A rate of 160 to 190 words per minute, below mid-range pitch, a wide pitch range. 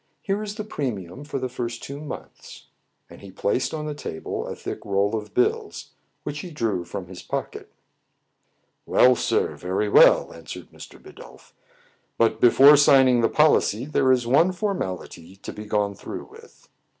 Yes: average, 175 wpm; low, 125 Hz; wide, 6.5 semitones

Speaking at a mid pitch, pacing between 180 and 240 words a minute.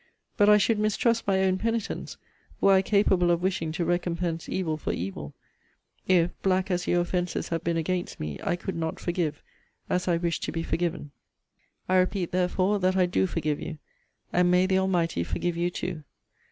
Yes: medium, 180 Hz; average, 185 wpm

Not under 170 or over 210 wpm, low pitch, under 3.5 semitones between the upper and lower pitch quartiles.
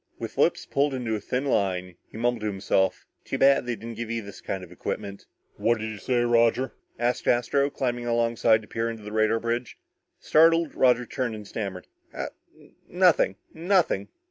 Yes: average, 180 wpm; low, 115 Hz; average, 2.7 semitones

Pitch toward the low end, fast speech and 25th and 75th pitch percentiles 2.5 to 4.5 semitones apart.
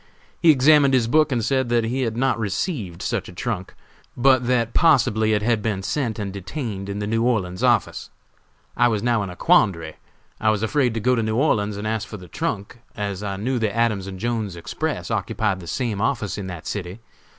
Yes: low, 110 Hz; fast, 215 wpm; average, 3.6 semitones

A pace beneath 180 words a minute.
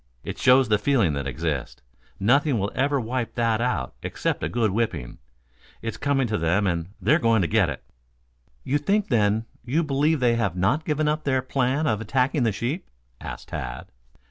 No: average, 190 wpm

